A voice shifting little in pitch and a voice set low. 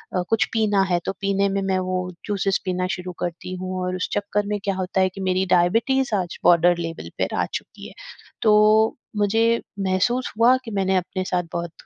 No: narrow, 2.3 semitones; high, 190 Hz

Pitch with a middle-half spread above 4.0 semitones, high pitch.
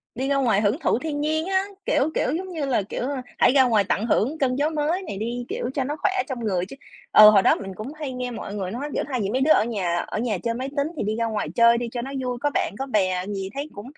Yes: average, 5.1 semitones; high, 245 Hz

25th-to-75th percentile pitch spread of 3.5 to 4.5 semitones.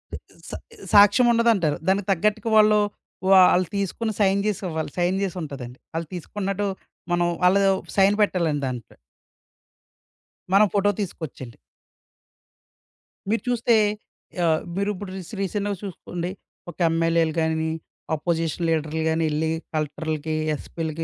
Yes: average, 4.1 semitones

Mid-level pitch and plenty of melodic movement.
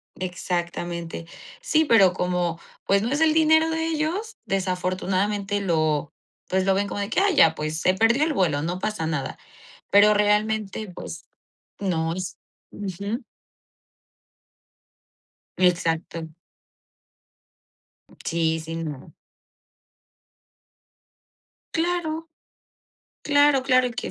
No: high, 195 Hz; wide, 7.1 semitones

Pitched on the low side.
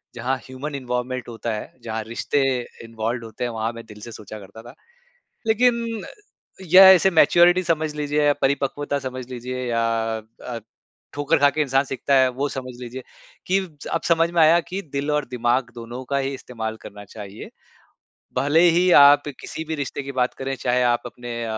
Yes: low, 130 Hz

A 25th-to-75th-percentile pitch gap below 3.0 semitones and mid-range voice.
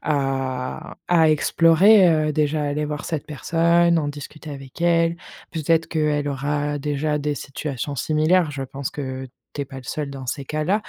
Yes: narrow, 2.6 semitones; medium, 150 Hz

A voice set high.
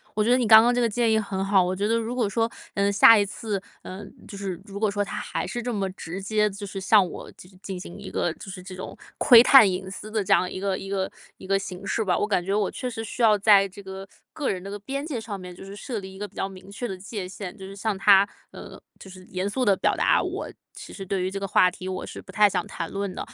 Yes: high, 200 Hz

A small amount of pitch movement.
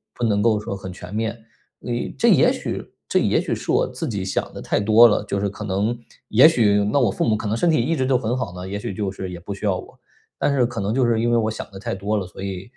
No: average, 3.3 semitones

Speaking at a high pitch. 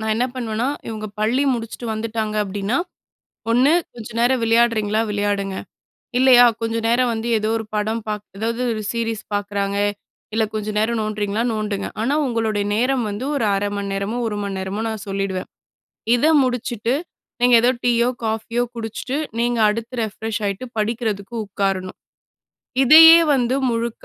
Yes: high, 225 Hz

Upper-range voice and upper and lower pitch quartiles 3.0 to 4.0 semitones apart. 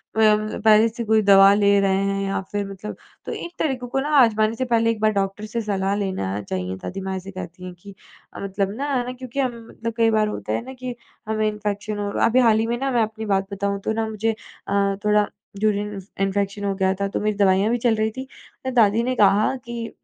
No: high, 210 Hz; narrow, 2.4 semitones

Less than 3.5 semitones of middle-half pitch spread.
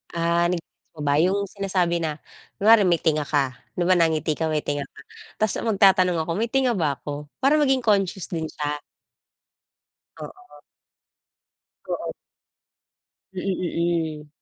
No: average, 4.2 semitones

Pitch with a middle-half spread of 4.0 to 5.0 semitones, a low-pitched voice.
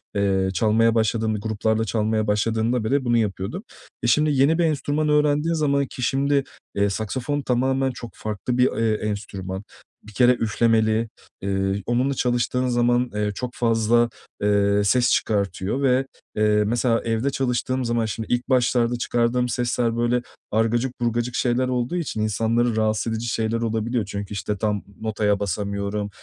No: average, 2.8 semitones; low, 115 Hz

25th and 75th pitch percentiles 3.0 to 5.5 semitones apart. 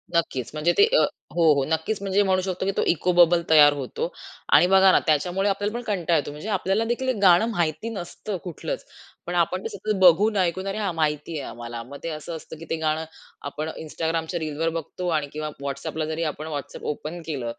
Yes: average, 4.0 semitones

